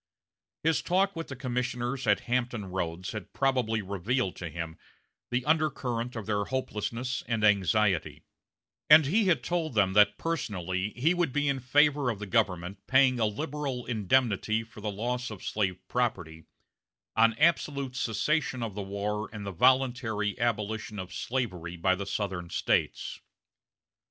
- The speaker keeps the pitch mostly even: No, average, 4.6 semitones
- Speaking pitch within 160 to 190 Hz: No, low, 115 Hz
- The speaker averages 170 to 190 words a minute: No, average, 150 wpm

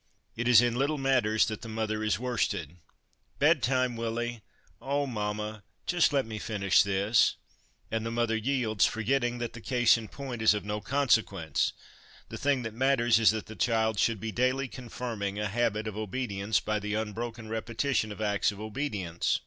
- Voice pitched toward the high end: No, low, 110 Hz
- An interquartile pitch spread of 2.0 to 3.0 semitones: Yes, narrow, 2.4 semitones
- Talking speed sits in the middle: Yes, average, 190 wpm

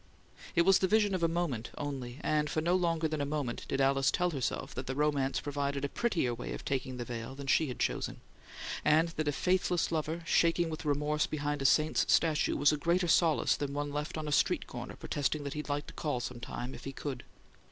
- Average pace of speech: No, fast, 230 wpm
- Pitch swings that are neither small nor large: Yes, average, 3.1 semitones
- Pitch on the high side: No, medium, 150 Hz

